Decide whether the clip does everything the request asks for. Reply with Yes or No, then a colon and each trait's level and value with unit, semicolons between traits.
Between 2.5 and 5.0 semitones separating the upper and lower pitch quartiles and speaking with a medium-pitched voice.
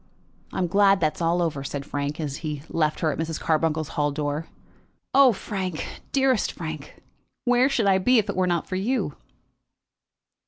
Yes: average, 4.7 semitones; medium, 165 Hz